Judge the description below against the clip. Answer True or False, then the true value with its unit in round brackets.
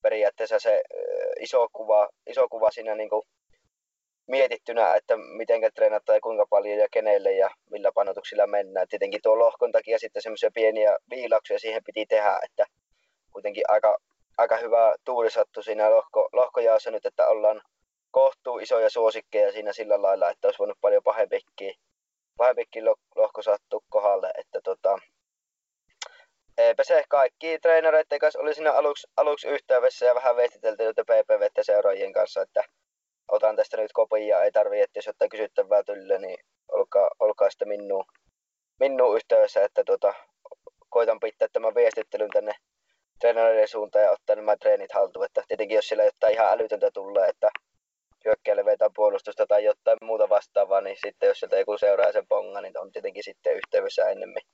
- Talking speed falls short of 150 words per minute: False (155 wpm)